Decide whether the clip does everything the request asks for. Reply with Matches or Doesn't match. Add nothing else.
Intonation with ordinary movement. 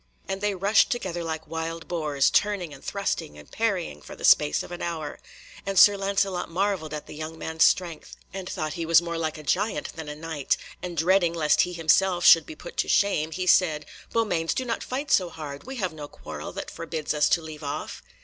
Matches